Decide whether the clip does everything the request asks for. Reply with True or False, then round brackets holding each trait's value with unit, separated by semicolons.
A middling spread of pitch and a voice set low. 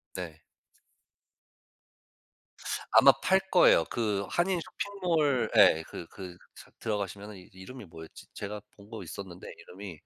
False (5.8 semitones; 100 Hz)